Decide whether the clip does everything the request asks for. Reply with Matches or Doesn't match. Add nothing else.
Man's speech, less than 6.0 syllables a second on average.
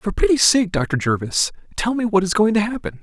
Matches